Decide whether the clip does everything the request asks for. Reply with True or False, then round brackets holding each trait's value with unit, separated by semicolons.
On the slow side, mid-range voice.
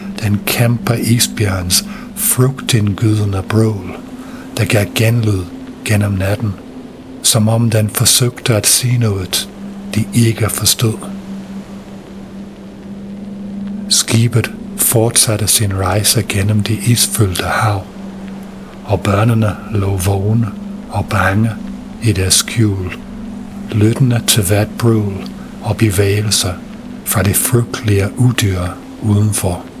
False (95 wpm; 115 Hz)